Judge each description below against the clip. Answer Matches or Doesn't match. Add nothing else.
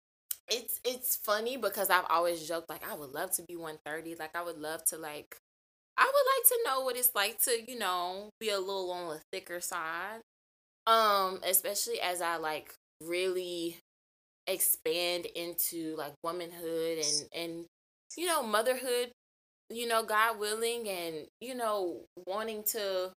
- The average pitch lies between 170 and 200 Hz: Matches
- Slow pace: Doesn't match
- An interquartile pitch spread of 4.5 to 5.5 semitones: Matches